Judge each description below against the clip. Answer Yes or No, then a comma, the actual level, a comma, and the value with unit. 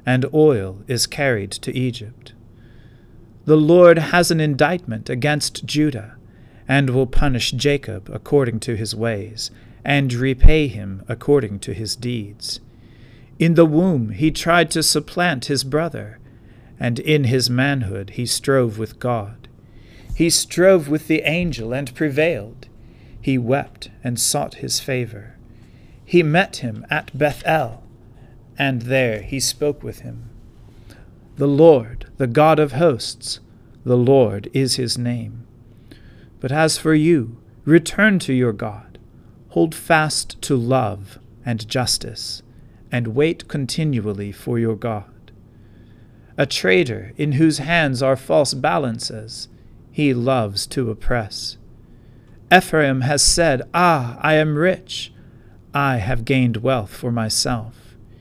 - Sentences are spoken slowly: Yes, slow, 130 wpm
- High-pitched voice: No, low, 125 Hz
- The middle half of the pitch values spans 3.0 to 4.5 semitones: Yes, average, 4.0 semitones